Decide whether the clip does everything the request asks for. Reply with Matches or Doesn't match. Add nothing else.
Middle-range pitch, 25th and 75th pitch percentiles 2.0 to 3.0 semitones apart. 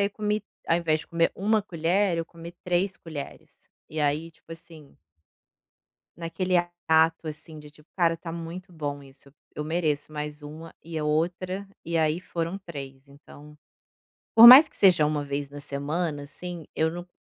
Matches